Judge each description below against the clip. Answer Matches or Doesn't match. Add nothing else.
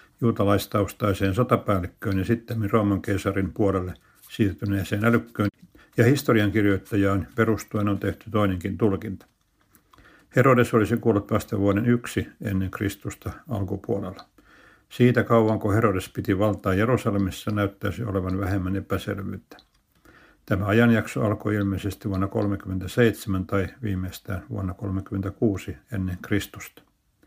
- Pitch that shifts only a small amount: Matches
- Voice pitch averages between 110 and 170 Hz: Doesn't match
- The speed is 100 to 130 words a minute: Matches